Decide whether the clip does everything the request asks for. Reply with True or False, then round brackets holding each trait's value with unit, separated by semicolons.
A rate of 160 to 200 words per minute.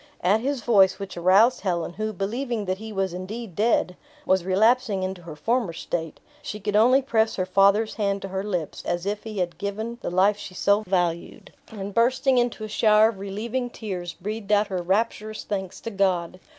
True (195 wpm)